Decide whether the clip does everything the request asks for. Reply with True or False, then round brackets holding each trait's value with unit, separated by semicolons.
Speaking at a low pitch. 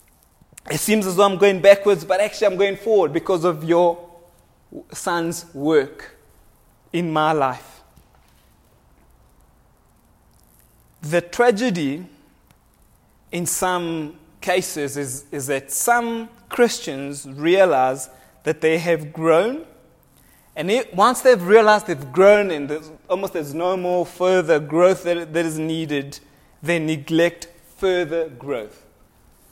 False (170 Hz)